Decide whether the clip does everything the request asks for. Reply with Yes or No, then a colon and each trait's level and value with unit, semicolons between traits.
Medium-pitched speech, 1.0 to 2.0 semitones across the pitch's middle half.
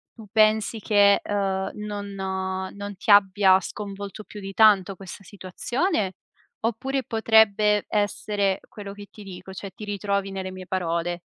No: high, 200 Hz; narrow, 1.7 semitones